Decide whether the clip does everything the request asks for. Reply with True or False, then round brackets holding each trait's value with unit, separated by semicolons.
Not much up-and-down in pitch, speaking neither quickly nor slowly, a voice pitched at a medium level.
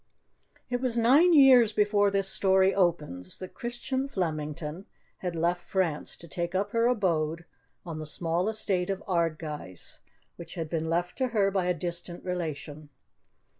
False (4.1 semitones; 155 wpm; 180 Hz)